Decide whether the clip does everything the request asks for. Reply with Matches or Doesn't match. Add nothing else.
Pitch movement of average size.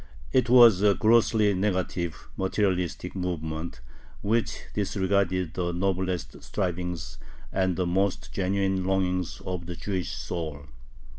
Doesn't match